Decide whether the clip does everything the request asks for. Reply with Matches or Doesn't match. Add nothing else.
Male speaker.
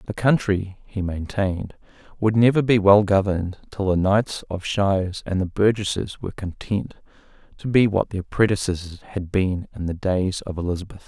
Matches